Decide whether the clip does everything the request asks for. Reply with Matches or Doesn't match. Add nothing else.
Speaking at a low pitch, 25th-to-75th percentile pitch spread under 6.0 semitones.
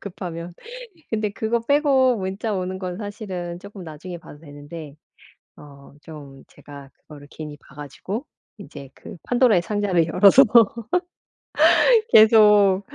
Doesn't match